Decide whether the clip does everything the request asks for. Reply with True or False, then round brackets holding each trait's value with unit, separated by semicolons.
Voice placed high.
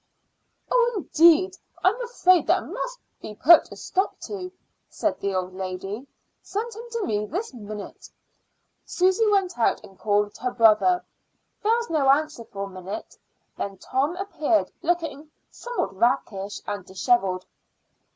True (285 Hz)